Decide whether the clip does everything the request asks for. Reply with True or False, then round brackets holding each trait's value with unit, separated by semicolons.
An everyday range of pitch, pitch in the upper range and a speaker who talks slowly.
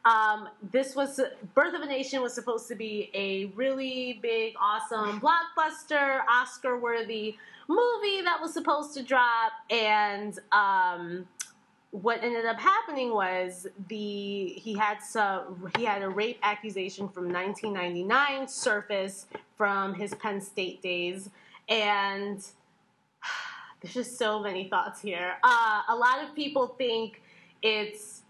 True (4.7 semitones; 220 Hz; 130 wpm)